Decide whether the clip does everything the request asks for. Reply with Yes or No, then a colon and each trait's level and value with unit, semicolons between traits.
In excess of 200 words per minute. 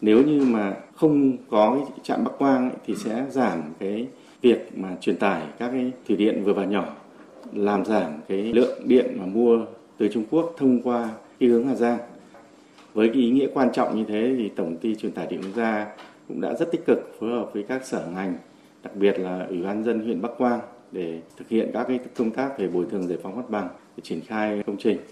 Yes: average, 225 wpm